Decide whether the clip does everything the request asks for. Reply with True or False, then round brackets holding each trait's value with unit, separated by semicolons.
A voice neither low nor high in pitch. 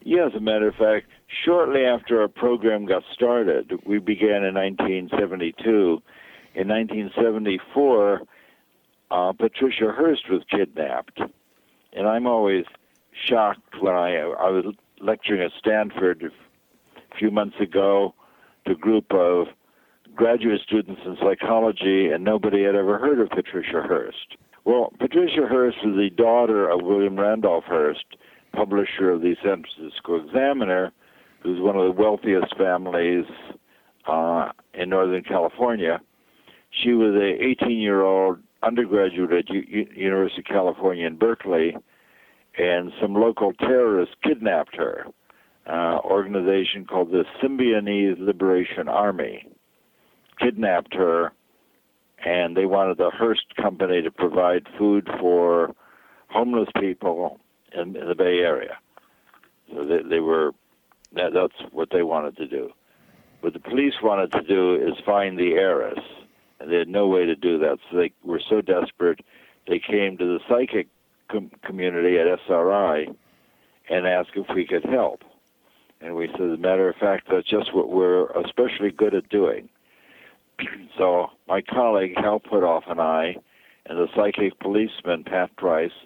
False (100 Hz)